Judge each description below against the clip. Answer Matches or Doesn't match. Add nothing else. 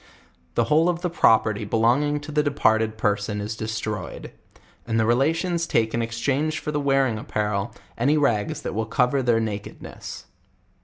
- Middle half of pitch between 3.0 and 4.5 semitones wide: Doesn't match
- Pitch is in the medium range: Doesn't match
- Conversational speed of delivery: Matches